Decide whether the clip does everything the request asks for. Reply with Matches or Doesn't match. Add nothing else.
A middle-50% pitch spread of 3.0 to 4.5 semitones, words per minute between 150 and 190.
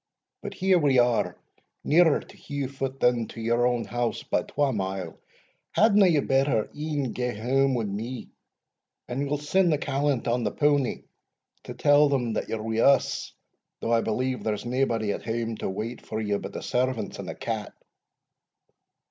Matches